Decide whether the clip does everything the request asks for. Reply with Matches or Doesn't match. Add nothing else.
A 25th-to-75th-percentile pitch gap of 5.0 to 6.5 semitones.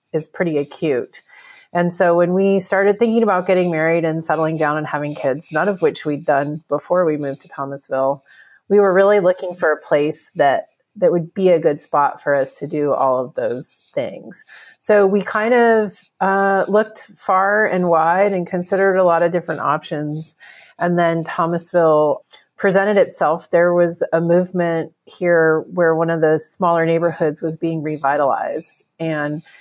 Doesn't match